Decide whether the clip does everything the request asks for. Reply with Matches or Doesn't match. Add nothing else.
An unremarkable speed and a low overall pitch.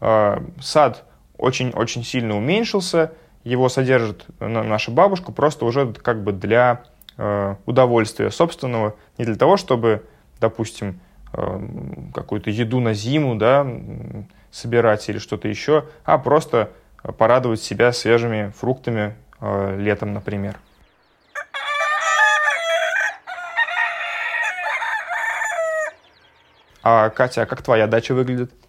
Doesn't match